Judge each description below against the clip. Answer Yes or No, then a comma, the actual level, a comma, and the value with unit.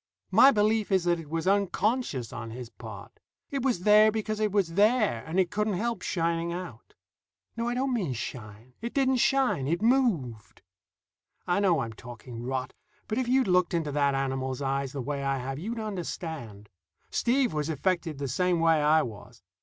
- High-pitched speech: No, medium, 170 Hz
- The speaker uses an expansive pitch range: Yes, wide, 7.9 semitones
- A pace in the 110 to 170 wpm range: No, average, 185 wpm